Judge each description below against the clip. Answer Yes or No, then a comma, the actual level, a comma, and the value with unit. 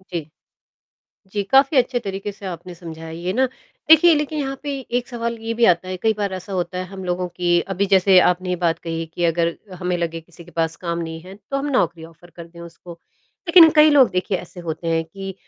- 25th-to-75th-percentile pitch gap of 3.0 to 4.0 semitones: No, average, 4.8 semitones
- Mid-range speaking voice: Yes, medium, 180 Hz